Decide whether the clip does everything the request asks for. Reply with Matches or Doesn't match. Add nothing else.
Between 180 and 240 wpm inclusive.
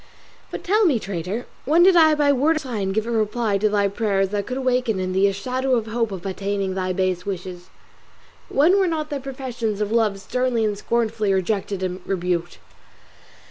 Matches